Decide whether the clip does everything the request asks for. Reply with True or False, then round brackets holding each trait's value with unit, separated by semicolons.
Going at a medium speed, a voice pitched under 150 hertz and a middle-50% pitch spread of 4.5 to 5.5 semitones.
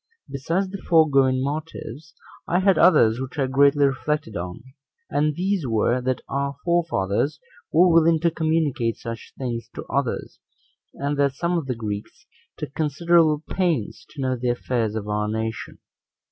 True (155 wpm; 140 Hz; 5.1 semitones)